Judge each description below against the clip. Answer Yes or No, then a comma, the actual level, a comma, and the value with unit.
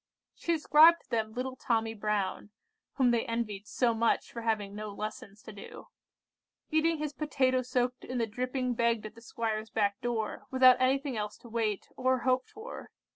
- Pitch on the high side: Yes, high, 235 Hz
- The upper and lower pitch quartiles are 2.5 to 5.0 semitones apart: Yes, average, 3.1 semitones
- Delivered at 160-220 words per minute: Yes, average, 175 wpm